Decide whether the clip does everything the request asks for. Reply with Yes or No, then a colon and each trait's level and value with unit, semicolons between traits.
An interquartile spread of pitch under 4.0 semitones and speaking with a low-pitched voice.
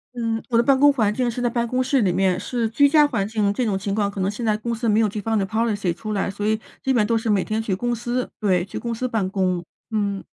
No: average, 3.0 semitones; high, 220 Hz